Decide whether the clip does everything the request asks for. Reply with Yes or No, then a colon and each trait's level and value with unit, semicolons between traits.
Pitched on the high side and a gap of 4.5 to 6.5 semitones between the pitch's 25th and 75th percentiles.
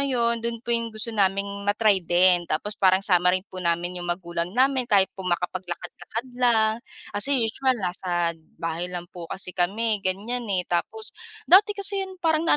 Yes: high, 200 Hz; average, 4.8 semitones